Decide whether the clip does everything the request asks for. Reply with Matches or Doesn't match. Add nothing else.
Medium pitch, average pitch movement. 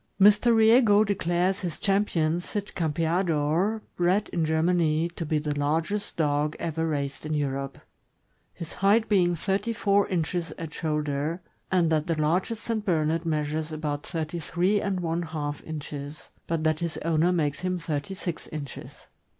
Matches